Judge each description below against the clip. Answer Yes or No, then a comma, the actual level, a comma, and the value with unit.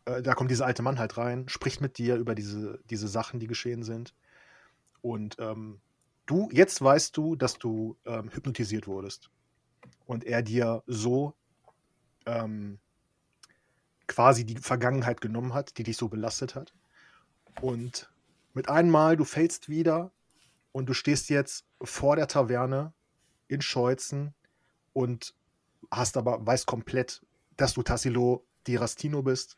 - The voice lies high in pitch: No, low, 125 Hz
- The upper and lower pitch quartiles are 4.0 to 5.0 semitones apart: No, average, 3.1 semitones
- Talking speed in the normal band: Yes, average, 140 wpm